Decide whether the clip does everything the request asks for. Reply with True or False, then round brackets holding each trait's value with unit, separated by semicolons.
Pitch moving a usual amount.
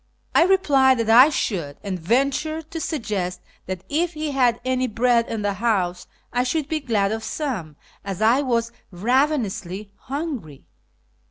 False (6.0 semitones)